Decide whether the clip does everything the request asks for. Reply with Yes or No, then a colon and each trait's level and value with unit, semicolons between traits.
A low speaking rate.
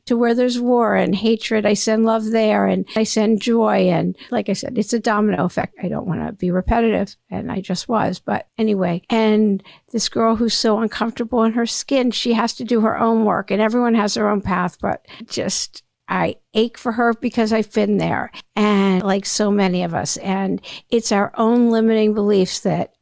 No: fast, 205 wpm